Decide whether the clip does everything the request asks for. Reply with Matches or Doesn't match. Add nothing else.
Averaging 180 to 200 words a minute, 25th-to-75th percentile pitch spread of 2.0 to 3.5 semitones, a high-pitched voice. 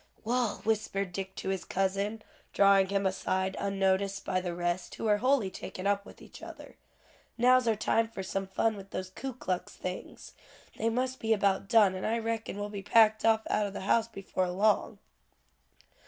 Matches